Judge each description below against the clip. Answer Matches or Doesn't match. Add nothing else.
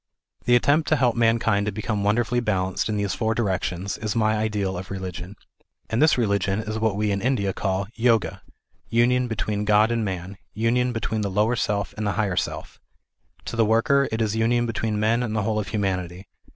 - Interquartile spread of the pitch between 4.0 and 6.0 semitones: Doesn't match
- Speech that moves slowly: Doesn't match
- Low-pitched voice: Matches